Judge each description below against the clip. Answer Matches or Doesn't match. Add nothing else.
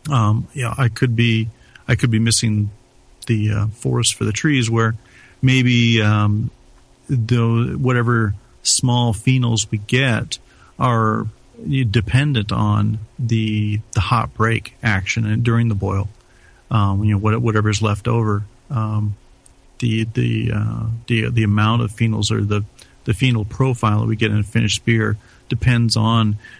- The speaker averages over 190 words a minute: Doesn't match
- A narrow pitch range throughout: Matches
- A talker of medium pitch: Doesn't match